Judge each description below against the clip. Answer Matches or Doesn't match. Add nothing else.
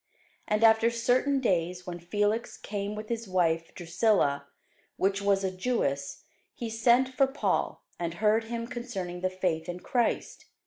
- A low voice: Doesn't match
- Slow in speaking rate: Doesn't match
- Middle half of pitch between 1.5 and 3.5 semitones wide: Doesn't match